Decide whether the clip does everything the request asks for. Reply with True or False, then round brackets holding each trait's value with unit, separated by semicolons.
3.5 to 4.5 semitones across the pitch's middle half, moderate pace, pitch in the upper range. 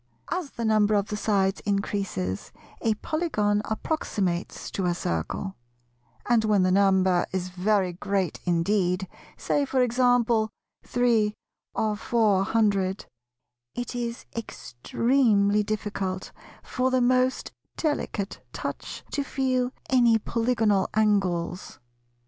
False (4.0 semitones; 115 wpm; 210 Hz)